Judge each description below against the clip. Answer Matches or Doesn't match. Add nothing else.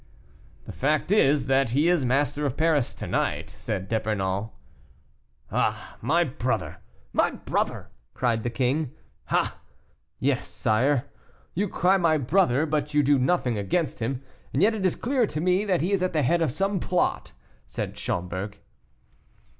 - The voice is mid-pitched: Matches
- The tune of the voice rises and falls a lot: Matches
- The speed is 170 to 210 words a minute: Doesn't match